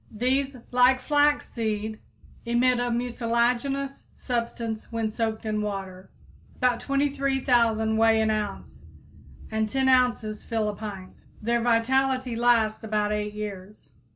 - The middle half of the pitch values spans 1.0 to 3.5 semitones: Yes, average, 2.8 semitones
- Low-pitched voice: No, high, 230 Hz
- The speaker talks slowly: Yes, slow, 120 wpm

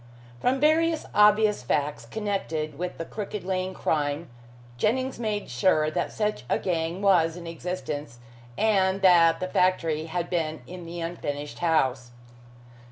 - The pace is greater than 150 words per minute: No, average, 140 wpm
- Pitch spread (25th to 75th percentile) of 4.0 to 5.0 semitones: Yes, average, 4.5 semitones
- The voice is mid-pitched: Yes, medium, 175 Hz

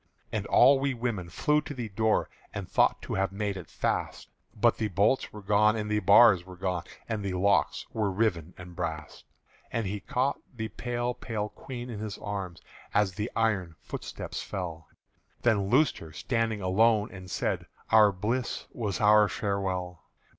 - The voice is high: No, low, 105 Hz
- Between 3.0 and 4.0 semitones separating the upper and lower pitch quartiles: Yes, average, 3.4 semitones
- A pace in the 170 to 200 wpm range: Yes, average, 175 wpm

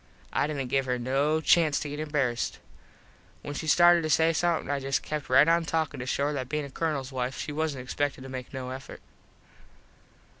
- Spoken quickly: Yes, fast, 215 wpm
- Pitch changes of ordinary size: Yes, average, 3.0 semitones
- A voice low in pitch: No, medium, 145 Hz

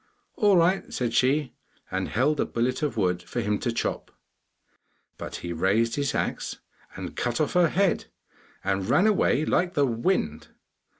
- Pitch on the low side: Yes, low, 130 Hz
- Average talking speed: Yes, average, 165 wpm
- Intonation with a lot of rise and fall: Yes, wide, 7.0 semitones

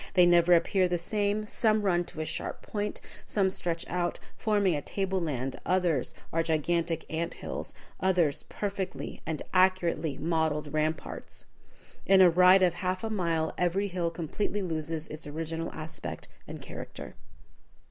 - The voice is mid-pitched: Yes, medium, 175 Hz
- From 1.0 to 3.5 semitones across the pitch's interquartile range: Yes, average, 2.9 semitones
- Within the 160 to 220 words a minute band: No, average, 150 wpm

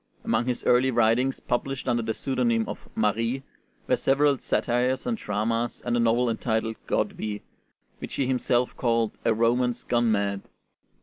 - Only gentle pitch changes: Yes, narrow, 2.0 semitones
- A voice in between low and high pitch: No, low, 120 Hz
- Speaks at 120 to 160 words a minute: Yes, average, 150 wpm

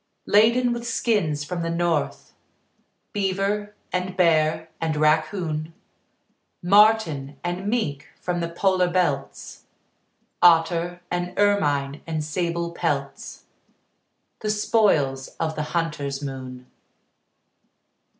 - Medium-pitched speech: Yes, medium, 170 Hz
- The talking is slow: Yes, slow, 100 wpm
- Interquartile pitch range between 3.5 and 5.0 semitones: Yes, average, 4.3 semitones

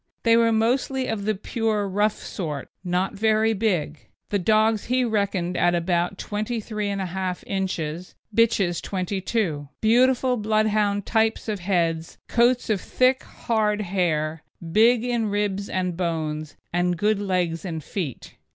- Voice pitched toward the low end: No, high, 200 Hz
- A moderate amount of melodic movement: Yes, average, 3.9 semitones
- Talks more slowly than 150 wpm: Yes, slow, 135 wpm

